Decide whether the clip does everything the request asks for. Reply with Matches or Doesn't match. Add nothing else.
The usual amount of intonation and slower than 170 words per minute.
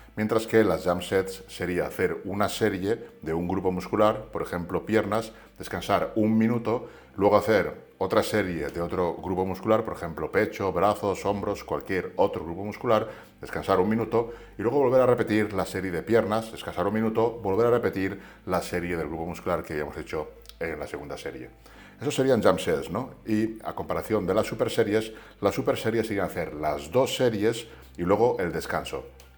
Doesn't match